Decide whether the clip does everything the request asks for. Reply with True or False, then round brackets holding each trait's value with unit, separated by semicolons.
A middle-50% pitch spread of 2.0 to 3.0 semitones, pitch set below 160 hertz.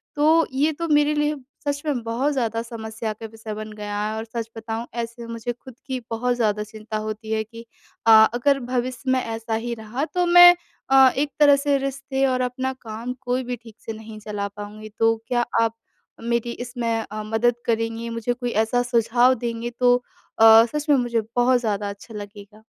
False (2.7 semitones; 235 Hz)